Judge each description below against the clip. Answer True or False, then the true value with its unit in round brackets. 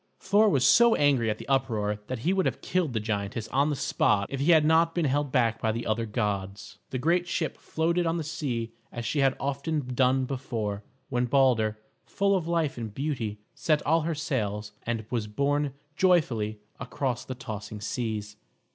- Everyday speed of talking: True (190 wpm)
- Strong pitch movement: True (5.8 semitones)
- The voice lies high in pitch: False (130 Hz)